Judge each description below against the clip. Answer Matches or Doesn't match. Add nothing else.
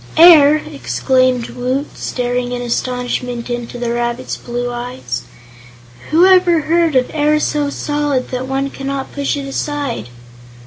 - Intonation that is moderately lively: Matches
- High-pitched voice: Matches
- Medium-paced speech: Doesn't match